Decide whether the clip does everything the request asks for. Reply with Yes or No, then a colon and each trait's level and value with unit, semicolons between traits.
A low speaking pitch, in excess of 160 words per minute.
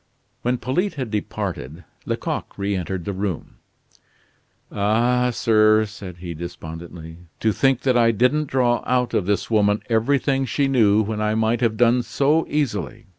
No: low, 110 Hz; average, 150 wpm